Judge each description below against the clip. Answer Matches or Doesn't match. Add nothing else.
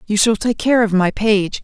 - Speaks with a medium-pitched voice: Doesn't match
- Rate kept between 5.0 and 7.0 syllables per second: Doesn't match